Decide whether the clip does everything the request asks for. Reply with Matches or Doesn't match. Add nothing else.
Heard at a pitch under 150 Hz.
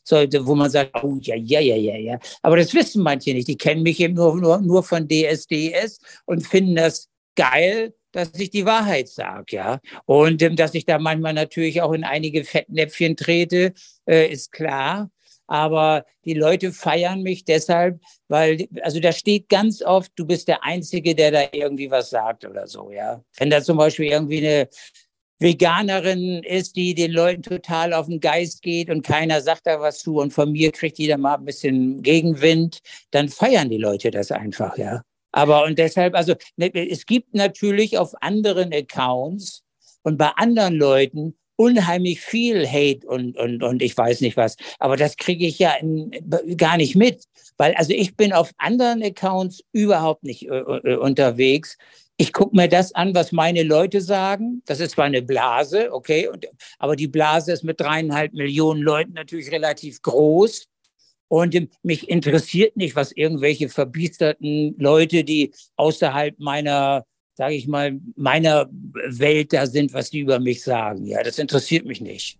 Doesn't match